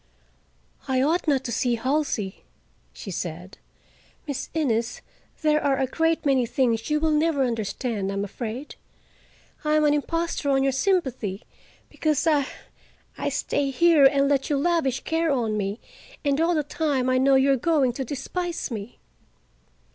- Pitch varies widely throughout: No, average, 4.0 semitones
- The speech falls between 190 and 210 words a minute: No, average, 160 wpm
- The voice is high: Yes, very high, 275 Hz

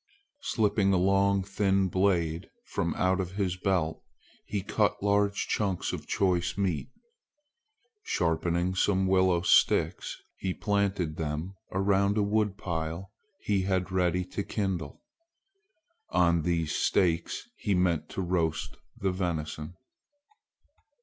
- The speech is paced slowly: Yes, slow, 115 wpm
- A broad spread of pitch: No, narrow, 2.4 semitones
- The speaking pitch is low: Yes, very low, 95 Hz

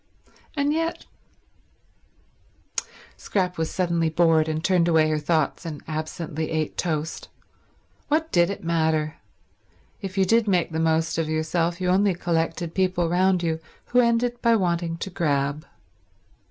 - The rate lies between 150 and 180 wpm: No, average, 140 wpm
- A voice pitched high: No, medium, 170 Hz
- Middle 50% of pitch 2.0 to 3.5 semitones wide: Yes, average, 2.9 semitones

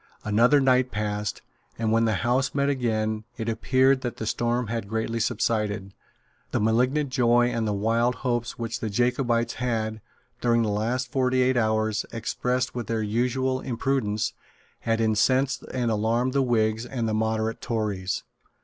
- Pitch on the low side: Yes, low, 115 Hz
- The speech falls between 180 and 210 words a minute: No, average, 160 wpm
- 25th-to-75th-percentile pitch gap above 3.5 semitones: No, narrow, 2.4 semitones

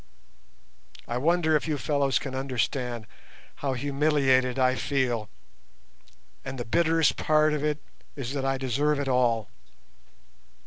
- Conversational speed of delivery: No, slow, 130 wpm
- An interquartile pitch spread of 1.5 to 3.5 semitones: Yes, average, 2.8 semitones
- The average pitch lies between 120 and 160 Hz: Yes, low, 135 Hz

